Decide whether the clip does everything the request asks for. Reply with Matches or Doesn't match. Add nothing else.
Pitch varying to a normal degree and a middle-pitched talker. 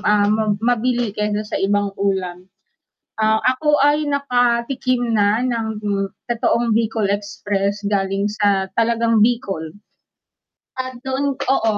Doesn't match